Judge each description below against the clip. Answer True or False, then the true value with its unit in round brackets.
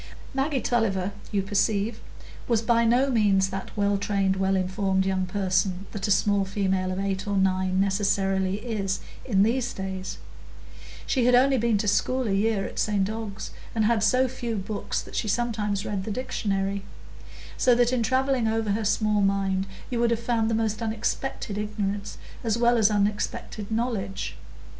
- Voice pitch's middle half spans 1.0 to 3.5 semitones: True (3.0 semitones)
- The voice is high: True (205 Hz)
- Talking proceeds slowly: False (170 wpm)